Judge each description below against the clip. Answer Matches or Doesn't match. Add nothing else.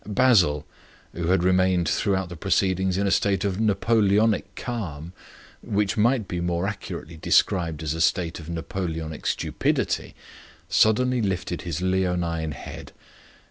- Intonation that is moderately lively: Matches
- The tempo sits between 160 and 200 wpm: Doesn't match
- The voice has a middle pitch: Doesn't match